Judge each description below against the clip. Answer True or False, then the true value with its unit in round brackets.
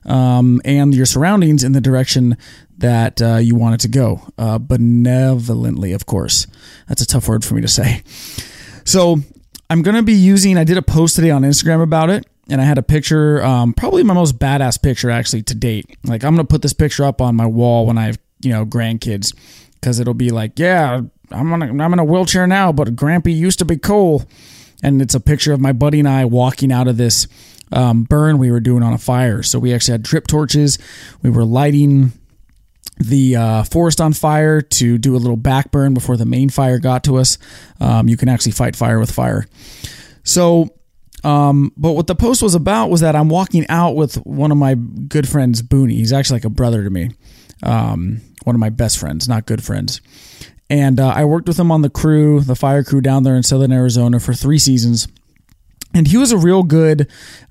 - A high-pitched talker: False (130 Hz)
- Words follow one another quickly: True (215 wpm)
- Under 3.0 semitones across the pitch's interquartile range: False (4.2 semitones)